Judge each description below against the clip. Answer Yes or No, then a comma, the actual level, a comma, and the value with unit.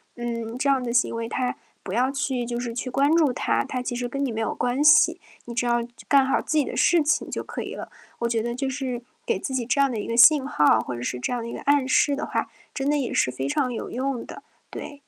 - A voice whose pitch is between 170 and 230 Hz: No, very high, 250 Hz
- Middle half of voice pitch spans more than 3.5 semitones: No, average, 2.8 semitones